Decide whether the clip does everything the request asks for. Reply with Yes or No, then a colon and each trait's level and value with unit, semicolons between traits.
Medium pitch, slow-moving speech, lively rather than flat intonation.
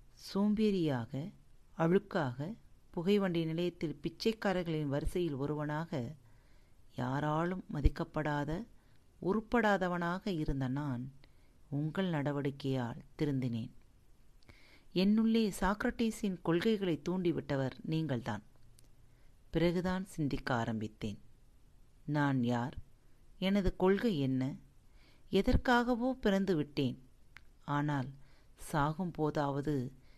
Yes: medium, 150 Hz; slow, 65 wpm; wide, 6.3 semitones